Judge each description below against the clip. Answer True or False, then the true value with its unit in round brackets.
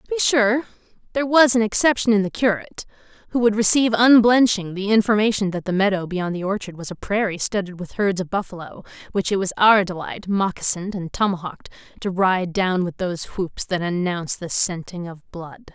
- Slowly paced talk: False (190 wpm)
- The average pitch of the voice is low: False (195 Hz)